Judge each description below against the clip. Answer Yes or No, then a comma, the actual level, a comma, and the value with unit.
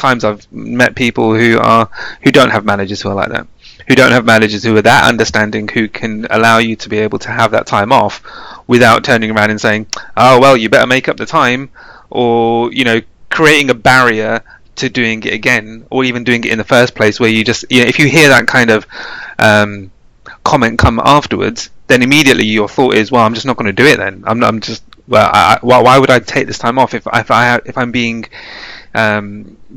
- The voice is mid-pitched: No, low, 115 Hz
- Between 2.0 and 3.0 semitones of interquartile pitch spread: Yes, narrow, 2.4 semitones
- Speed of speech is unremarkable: No, fast, 235 wpm